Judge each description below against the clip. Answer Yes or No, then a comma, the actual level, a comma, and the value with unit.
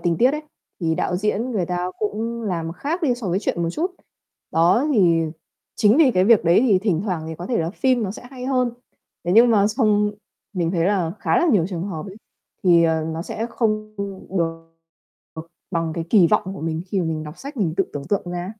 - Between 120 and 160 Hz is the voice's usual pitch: No, high, 190 Hz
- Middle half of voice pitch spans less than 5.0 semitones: No, average, 5.3 semitones